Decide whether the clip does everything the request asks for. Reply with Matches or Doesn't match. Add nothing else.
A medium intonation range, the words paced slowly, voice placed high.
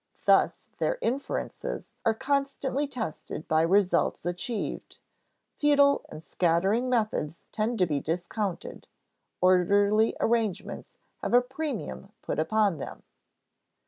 Doesn't match